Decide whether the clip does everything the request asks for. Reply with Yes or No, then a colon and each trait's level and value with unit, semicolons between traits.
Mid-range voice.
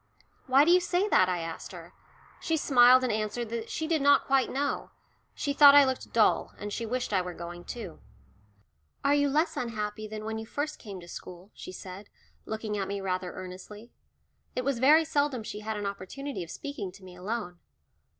No: high, 220 Hz